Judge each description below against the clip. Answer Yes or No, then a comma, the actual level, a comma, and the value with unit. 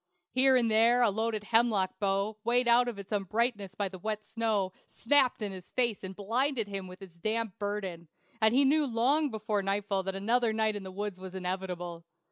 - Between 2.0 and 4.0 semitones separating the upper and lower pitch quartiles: Yes, average, 3.4 semitones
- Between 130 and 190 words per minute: No, average, 200 wpm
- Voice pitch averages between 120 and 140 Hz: No, high, 210 Hz